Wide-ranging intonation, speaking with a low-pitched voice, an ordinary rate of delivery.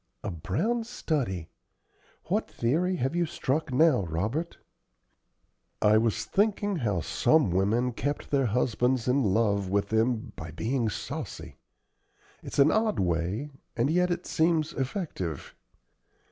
No: wide, 7.7 semitones; low, 125 Hz; slow, 130 wpm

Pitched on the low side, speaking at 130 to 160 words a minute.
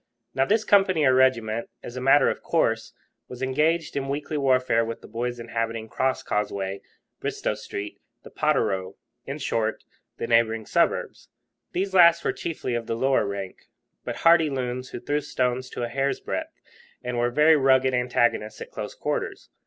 No: low, 125 Hz; average, 170 wpm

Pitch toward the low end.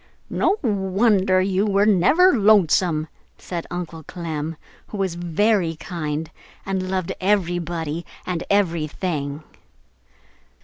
No: medium, 180 Hz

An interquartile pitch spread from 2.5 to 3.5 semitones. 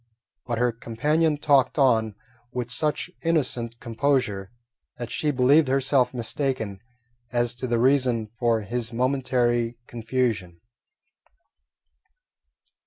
Yes: average, 2.8 semitones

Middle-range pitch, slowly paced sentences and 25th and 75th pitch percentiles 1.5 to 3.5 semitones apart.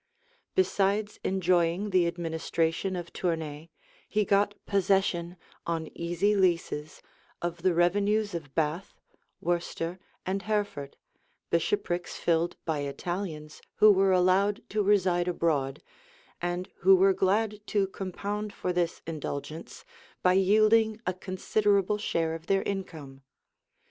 Yes: medium, 180 Hz; slow, 120 wpm; average, 3.1 semitones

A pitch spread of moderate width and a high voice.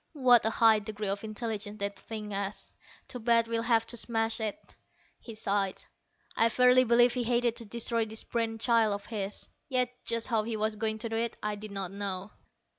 No: narrow, 1.9 semitones; high, 225 Hz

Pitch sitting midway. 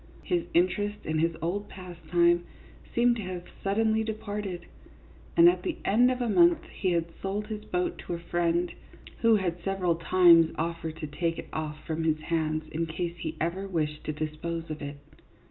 Yes: medium, 175 Hz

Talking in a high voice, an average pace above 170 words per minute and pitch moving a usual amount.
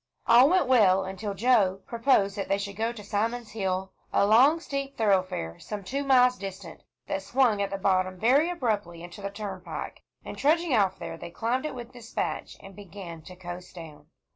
Yes: high, 205 Hz; average, 190 wpm; average, 4.7 semitones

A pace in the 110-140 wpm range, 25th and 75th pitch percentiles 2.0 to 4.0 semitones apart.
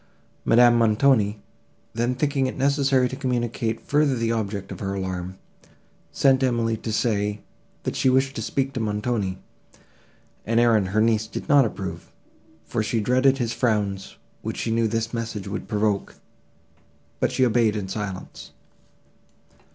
No: average, 150 wpm; average, 3.4 semitones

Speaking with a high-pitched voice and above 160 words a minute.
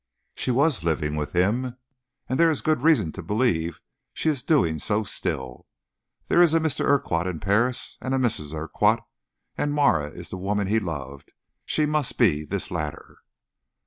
No: low, 105 Hz; average, 175 wpm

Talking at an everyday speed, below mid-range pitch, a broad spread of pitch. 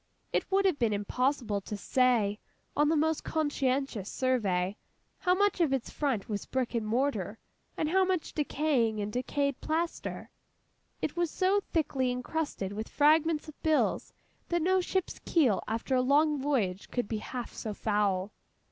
No: average, 160 wpm; very high, 265 Hz; wide, 6.3 semitones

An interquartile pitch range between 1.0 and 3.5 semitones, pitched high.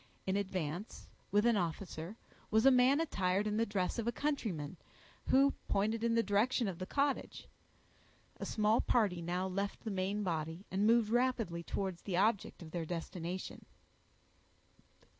No: average, 4.1 semitones; high, 200 Hz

